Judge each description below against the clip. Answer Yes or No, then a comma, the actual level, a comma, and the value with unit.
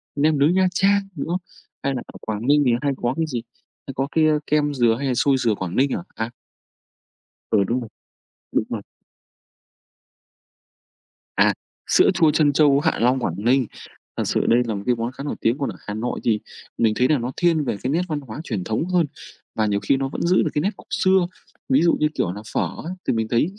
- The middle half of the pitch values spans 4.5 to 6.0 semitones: Yes, average, 5.0 semitones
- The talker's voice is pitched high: No, low, 135 Hz